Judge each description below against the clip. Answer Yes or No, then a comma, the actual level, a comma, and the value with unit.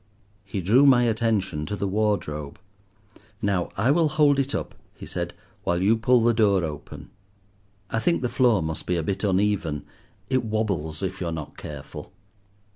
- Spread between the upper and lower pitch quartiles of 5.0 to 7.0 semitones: Yes, wide, 5.4 semitones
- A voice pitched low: Yes, low, 100 Hz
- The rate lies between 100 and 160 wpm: No, average, 175 wpm